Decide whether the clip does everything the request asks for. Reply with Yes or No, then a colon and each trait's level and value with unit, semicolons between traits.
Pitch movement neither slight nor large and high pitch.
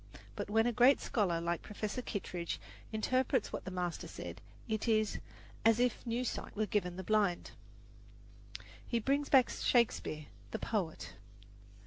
Yes: average, 4.7 semitones; high, 215 Hz